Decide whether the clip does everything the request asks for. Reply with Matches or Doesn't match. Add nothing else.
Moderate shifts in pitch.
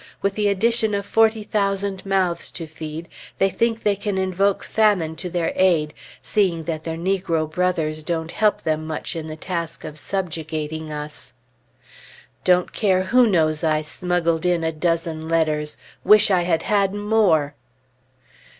Matches